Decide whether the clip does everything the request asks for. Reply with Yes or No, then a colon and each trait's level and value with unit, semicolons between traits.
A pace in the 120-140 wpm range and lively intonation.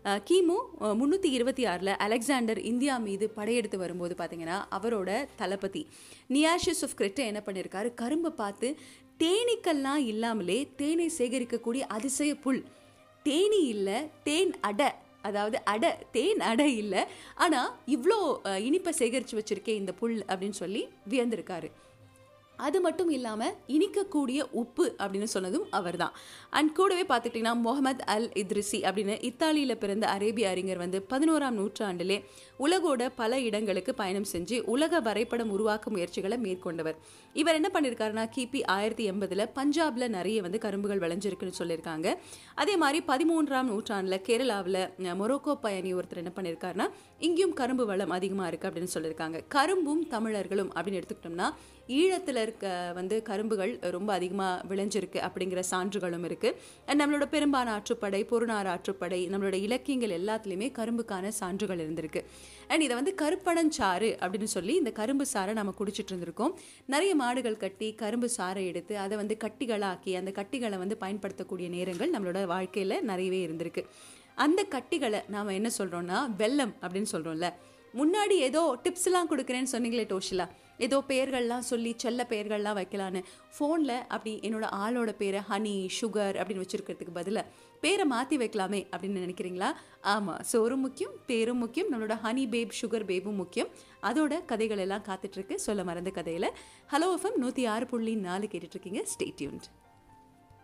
Yes: fast, 130 wpm; wide, 6.1 semitones